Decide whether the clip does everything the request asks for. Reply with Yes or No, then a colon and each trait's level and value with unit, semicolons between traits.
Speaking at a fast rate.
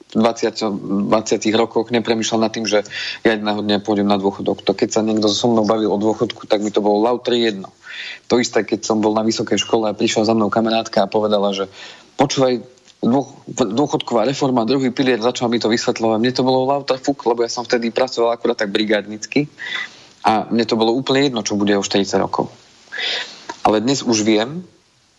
Yes: fast, 195 wpm